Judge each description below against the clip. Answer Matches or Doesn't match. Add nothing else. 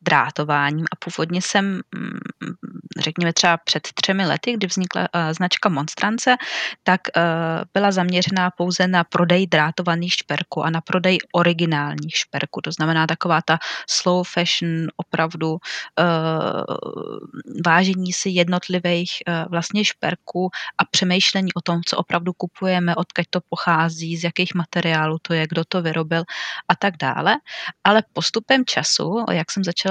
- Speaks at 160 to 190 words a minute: Doesn't match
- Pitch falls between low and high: Matches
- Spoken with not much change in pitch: Matches